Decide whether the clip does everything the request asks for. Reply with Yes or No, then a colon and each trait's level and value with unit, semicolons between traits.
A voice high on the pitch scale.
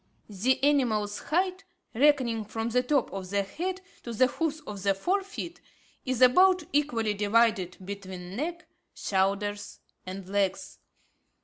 Yes: high, 230 Hz